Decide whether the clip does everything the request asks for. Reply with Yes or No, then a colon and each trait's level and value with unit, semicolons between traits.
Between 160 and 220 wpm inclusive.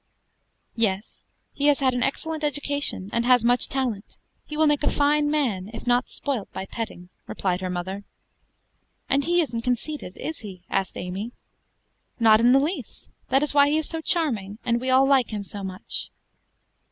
Yes: average, 180 wpm